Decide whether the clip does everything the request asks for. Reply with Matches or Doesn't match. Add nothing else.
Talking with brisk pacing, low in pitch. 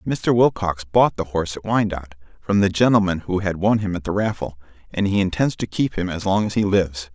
Matches